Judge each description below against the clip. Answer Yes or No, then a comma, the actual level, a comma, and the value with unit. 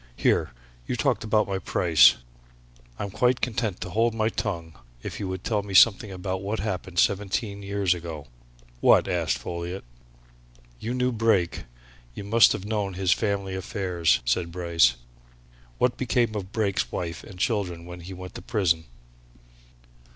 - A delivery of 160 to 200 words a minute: No, average, 150 wpm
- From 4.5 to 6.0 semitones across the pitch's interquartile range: No, average, 3.5 semitones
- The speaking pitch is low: Yes, very low, 95 Hz